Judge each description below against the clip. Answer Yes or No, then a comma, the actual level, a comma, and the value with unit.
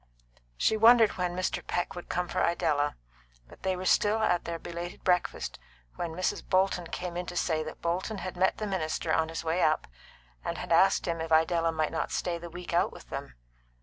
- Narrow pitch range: Yes, narrow, 2.0 semitones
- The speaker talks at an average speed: No, fast, 210 wpm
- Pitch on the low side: No, medium, 175 Hz